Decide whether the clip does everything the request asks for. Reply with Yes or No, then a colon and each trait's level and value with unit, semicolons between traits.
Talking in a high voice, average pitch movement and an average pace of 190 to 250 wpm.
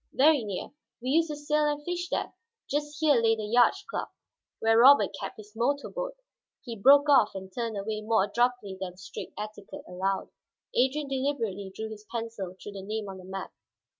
No: high, 230 Hz; wide, 5.9 semitones; average, 195 wpm